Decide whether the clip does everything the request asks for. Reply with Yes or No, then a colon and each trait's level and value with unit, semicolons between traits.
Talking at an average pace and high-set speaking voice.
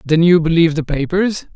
No: average, 195 wpm; medium, 165 Hz